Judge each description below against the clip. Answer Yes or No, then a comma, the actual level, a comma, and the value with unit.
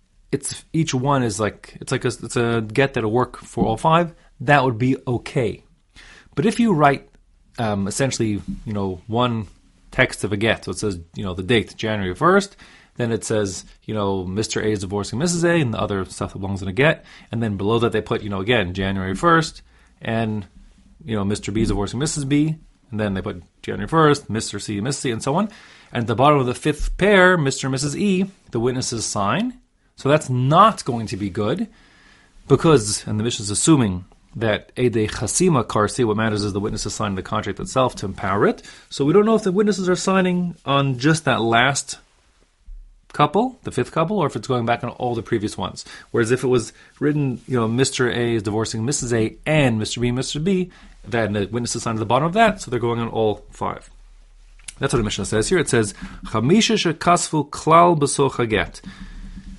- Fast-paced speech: Yes, fast, 215 wpm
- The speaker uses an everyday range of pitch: No, wide, 6.0 semitones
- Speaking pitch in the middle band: No, low, 120 Hz